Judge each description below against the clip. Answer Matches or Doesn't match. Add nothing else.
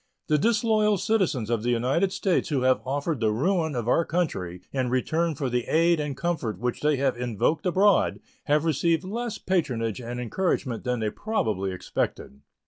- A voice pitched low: Doesn't match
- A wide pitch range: Matches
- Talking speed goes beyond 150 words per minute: Matches